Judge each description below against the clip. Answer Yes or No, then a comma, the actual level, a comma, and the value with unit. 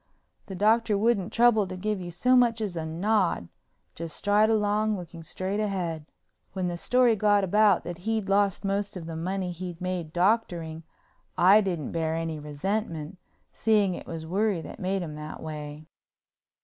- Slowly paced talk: No, average, 170 wpm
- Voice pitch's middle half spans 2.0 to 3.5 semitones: No, average, 4.0 semitones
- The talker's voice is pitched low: No, high, 190 Hz